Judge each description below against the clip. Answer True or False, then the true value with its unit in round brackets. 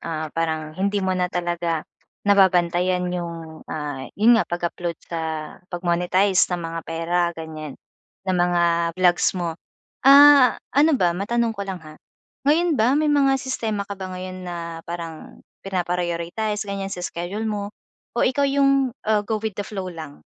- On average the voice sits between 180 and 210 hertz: True (185 Hz)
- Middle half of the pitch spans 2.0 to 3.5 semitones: False (4.2 semitones)